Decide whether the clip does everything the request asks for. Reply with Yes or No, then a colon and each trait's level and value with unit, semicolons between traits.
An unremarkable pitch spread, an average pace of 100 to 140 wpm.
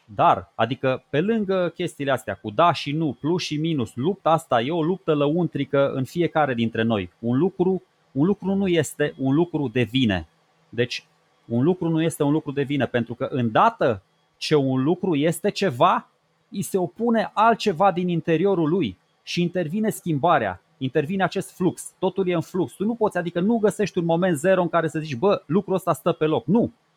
No: average, 4.9 semitones; fast, 195 wpm